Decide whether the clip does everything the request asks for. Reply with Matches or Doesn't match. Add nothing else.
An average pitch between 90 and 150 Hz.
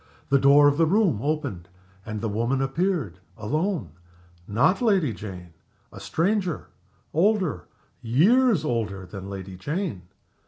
Matches